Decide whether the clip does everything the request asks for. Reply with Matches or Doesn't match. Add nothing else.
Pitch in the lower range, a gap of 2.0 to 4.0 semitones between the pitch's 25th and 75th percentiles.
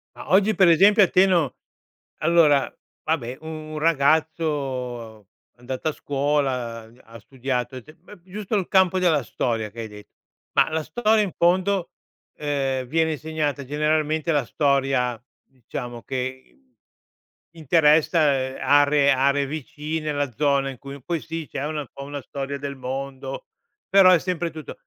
Doesn't match